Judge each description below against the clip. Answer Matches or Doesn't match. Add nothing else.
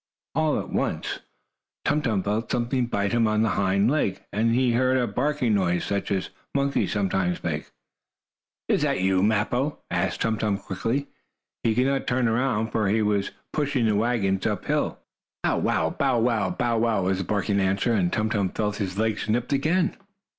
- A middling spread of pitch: Matches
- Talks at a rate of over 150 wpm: Matches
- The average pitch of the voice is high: Doesn't match